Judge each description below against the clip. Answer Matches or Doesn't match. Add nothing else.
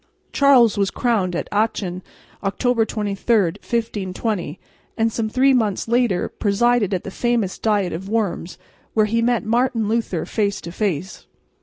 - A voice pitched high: Matches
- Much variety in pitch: Doesn't match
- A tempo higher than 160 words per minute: Doesn't match